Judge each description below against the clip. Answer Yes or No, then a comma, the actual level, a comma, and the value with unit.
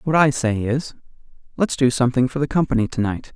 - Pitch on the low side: Yes, low, 130 Hz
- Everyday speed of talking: Yes, average, 195 wpm